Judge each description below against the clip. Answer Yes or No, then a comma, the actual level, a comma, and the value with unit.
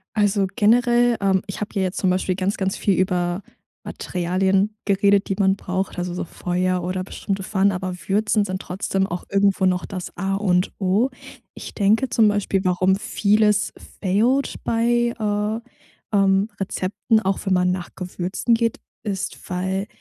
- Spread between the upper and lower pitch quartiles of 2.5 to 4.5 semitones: No, narrow, 2.1 semitones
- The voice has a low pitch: No, high, 195 Hz